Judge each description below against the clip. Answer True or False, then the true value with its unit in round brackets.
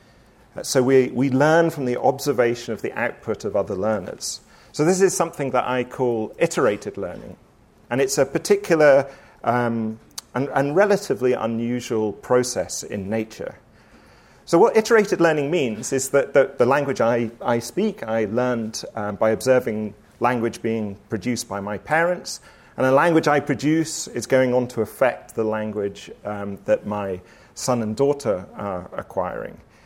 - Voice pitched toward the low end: True (125 Hz)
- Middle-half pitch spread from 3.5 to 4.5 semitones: True (4.2 semitones)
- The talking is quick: False (155 wpm)